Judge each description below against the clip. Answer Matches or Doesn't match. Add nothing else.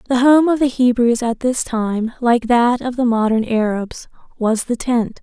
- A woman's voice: Matches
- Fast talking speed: Doesn't match